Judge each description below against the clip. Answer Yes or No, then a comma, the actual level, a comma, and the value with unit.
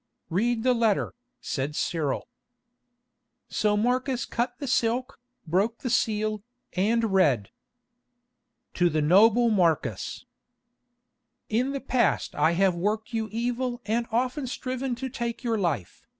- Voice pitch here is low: No, high, 225 Hz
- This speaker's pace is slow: Yes, slow, 125 wpm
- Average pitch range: Yes, average, 4.2 semitones